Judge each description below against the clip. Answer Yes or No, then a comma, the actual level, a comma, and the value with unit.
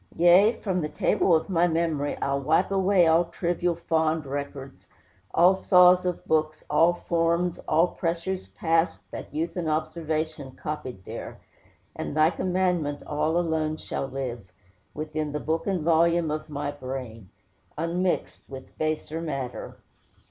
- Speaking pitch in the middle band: Yes, medium, 160 Hz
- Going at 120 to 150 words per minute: Yes, average, 140 wpm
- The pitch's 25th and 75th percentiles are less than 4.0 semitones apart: Yes, narrow, 2.6 semitones